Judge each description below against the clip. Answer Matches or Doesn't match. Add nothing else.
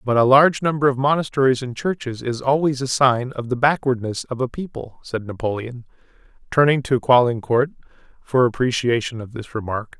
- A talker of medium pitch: Doesn't match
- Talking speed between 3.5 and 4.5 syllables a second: Doesn't match